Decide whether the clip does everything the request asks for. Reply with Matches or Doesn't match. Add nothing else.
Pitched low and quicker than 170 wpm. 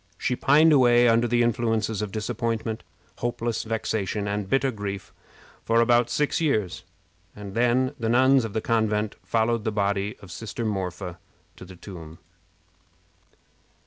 Doesn't match